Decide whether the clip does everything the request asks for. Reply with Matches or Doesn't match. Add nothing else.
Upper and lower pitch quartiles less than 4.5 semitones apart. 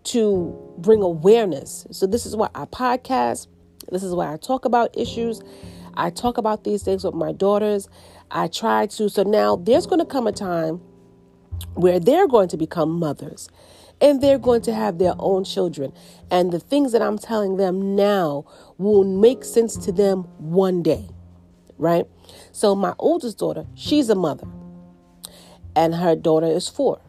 Doesn't match